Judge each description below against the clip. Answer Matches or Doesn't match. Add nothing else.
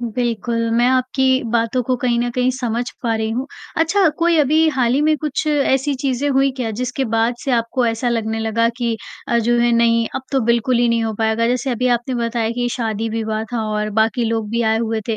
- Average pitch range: Doesn't match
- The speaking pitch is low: Doesn't match